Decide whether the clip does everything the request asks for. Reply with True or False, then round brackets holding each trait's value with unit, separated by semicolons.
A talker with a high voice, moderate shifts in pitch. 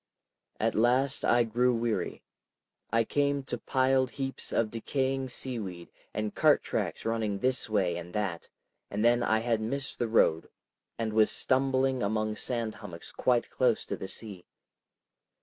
False (115 Hz; 3.4 semitones)